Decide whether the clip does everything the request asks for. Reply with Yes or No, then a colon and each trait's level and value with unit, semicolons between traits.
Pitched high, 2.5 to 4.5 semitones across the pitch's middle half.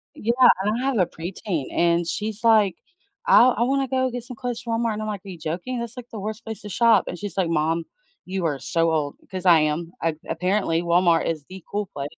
No: high, 195 Hz; wide, 5.4 semitones